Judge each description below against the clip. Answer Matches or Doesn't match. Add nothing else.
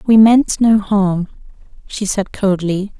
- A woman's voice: Matches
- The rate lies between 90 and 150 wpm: Matches